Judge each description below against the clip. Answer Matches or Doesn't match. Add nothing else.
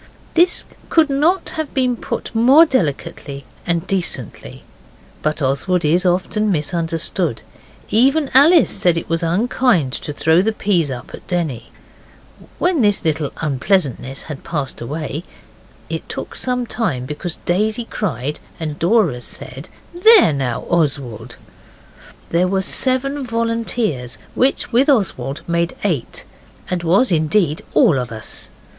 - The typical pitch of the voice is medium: Matches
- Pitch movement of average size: Doesn't match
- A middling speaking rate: Doesn't match